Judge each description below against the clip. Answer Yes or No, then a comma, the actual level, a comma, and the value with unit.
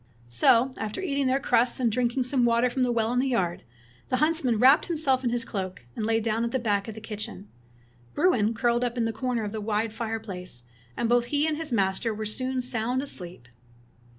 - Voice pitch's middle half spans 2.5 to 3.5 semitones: Yes, average, 3.0 semitones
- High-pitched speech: Yes, high, 235 Hz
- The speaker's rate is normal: No, fast, 235 wpm